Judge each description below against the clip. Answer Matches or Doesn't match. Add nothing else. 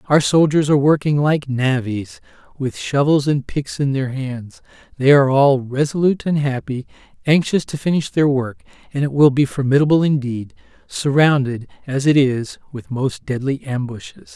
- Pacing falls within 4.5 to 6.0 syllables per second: Matches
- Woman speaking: Doesn't match